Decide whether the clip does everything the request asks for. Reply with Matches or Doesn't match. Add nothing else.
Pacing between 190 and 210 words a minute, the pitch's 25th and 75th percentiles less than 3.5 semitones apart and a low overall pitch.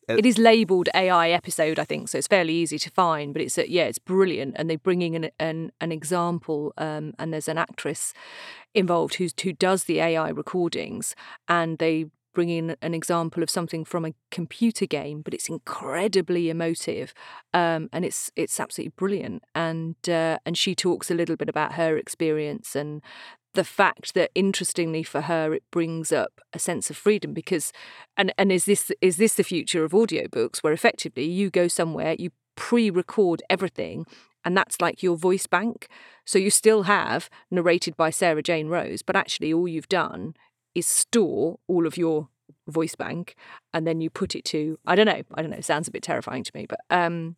Doesn't match